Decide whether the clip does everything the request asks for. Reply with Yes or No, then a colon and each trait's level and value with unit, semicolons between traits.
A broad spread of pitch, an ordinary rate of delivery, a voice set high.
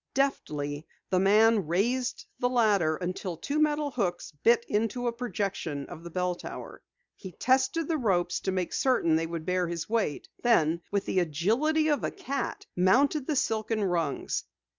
Yes: wide, 6.5 semitones; average, 165 wpm; high, 200 Hz